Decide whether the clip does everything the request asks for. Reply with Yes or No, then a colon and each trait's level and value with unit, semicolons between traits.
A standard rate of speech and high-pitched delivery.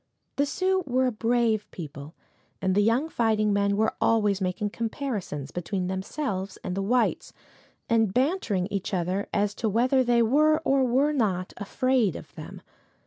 Yes: average, 160 wpm; high, 220 Hz